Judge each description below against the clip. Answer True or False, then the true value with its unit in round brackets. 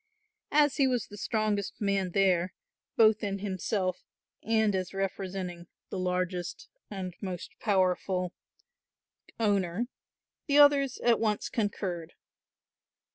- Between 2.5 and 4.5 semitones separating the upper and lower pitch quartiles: True (3.2 semitones)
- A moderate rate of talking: False (110 wpm)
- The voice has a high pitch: True (195 Hz)